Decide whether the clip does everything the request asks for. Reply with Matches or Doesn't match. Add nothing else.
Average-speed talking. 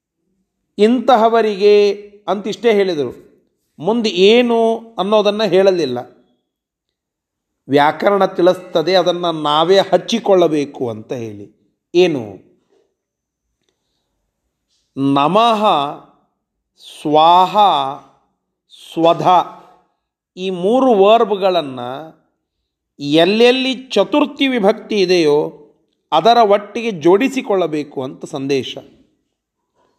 Doesn't match